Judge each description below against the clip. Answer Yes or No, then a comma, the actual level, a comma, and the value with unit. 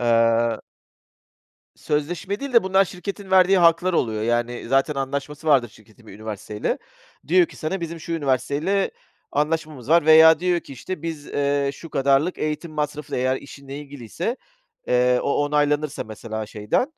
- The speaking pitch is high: No, medium, 145 Hz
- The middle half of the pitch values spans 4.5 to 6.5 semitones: Yes, average, 5.1 semitones